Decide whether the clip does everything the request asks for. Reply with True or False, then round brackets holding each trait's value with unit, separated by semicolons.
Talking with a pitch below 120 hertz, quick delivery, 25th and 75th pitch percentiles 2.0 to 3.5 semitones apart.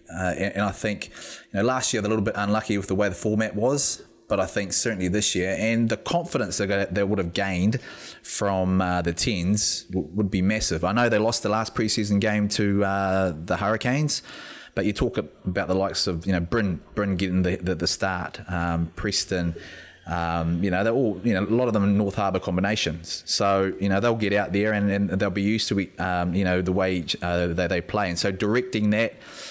True (100 Hz; 235 wpm; 2.6 semitones)